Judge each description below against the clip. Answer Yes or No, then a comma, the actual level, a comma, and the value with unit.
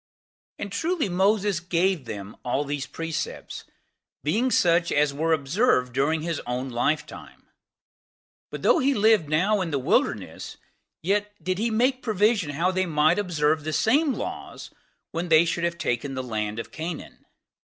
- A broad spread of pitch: Yes, wide, 5.9 semitones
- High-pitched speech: No, medium, 170 Hz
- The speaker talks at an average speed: Yes, average, 160 wpm